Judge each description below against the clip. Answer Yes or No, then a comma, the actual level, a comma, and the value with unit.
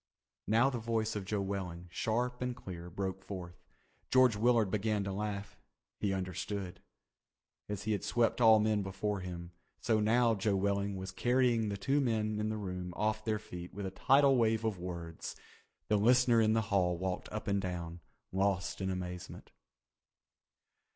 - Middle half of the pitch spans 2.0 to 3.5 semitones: Yes, average, 2.9 semitones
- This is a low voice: Yes, low, 100 Hz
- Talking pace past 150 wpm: Yes, average, 170 wpm